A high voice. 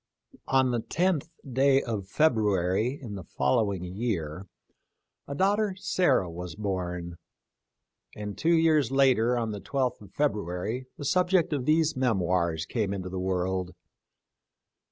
No: low, 110 Hz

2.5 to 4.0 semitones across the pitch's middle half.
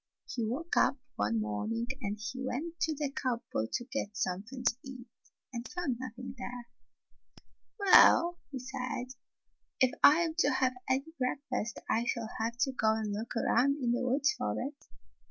Yes: average, 3.1 semitones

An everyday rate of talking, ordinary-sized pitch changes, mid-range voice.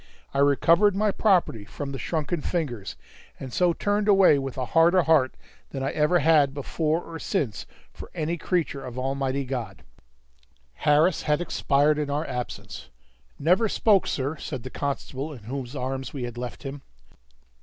Yes: average, 165 wpm; average, 4.0 semitones; medium, 145 Hz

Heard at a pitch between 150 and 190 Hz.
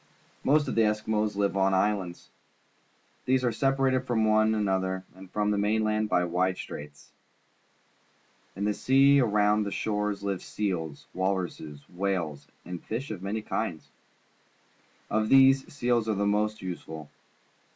No: low, 105 Hz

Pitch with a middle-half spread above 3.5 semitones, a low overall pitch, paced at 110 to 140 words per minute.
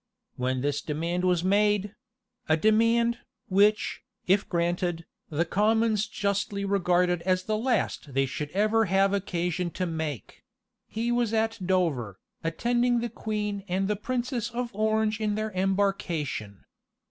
No: average, 4.0 semitones; high, 200 Hz; slow, 135 wpm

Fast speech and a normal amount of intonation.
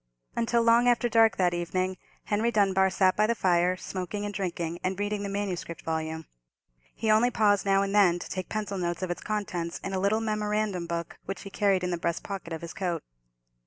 Yes: fast, 210 wpm; average, 3.1 semitones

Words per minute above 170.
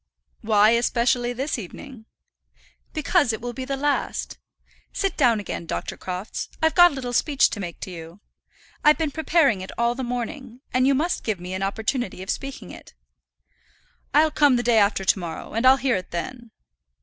Yes: average, 185 wpm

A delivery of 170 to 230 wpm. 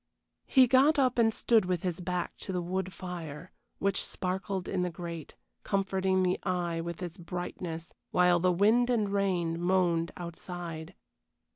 No: average, 155 wpm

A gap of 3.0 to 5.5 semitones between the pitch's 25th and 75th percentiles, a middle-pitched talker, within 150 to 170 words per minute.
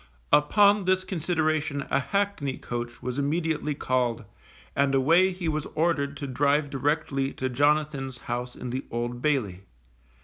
No: average, 3.6 semitones; medium, 145 Hz; average, 140 wpm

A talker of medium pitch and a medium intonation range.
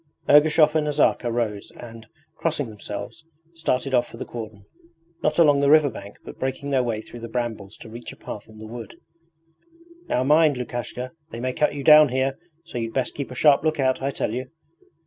No: low, 130 Hz; average, 4.0 semitones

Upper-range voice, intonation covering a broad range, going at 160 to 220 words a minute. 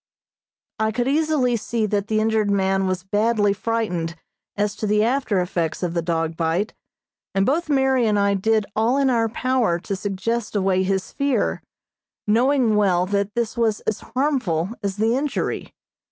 No: high, 215 Hz; average, 3.6 semitones; average, 170 wpm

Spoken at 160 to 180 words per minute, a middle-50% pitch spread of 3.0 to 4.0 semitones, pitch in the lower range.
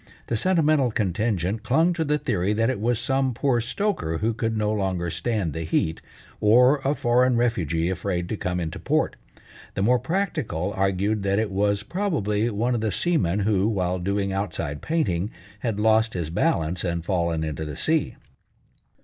No: average, 175 wpm; average, 5.3 semitones; low, 105 Hz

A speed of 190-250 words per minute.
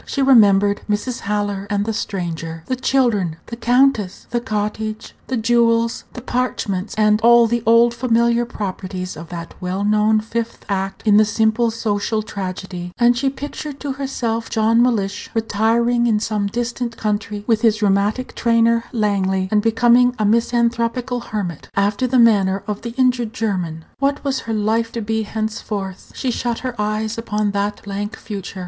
No: average, 165 wpm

